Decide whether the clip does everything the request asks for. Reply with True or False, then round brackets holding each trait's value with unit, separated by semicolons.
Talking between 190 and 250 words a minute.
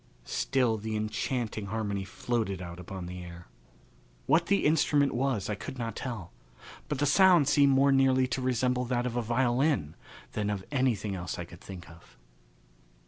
False (170 wpm)